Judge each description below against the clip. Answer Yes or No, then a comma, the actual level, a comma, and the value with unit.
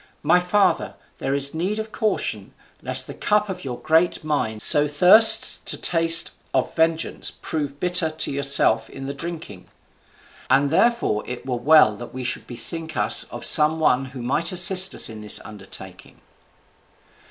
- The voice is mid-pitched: Yes, medium, 155 Hz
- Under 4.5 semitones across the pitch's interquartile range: No, wide, 5.4 semitones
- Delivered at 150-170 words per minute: Yes, average, 165 wpm